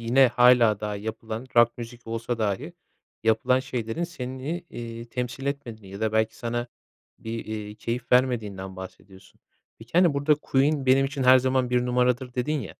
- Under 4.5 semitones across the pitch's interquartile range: Yes, average, 2.8 semitones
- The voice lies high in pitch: No, low, 120 Hz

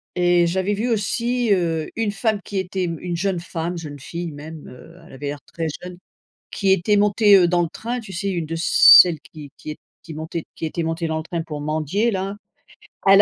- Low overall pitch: No, medium, 175 Hz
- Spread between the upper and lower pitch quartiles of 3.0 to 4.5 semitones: Yes, average, 3.6 semitones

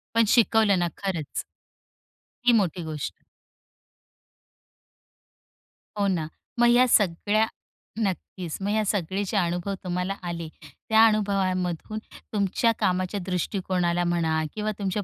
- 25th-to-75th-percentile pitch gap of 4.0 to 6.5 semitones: No, average, 3.3 semitones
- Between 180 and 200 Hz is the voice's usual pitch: Yes, high, 190 Hz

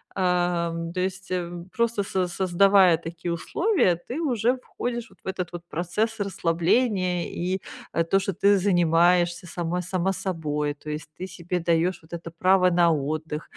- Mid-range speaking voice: Yes, medium, 180 Hz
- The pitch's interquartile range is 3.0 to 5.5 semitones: No, narrow, 2.4 semitones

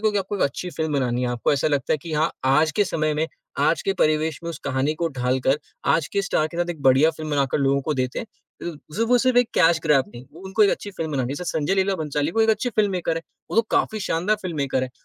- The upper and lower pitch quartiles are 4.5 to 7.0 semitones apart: Yes, wide, 5.4 semitones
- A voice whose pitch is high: No, medium, 155 Hz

